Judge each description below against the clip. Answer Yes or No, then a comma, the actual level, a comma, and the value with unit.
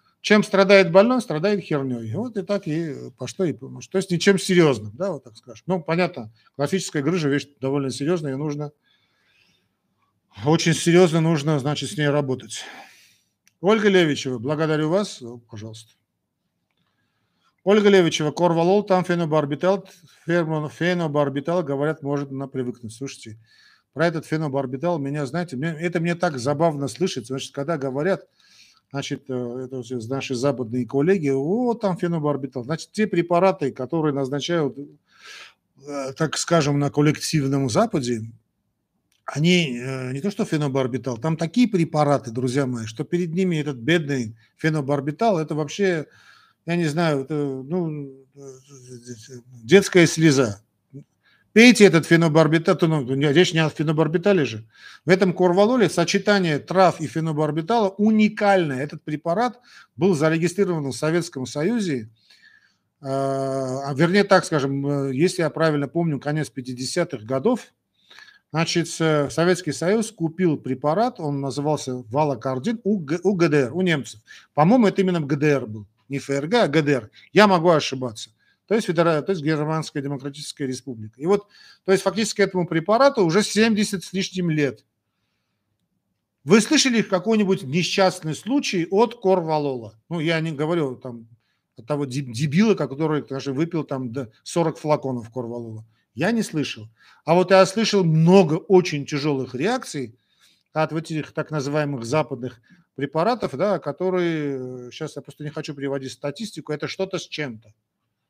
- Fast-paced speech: No, average, 135 wpm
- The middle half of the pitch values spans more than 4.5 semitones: Yes, average, 5.0 semitones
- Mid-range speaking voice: Yes, medium, 155 Hz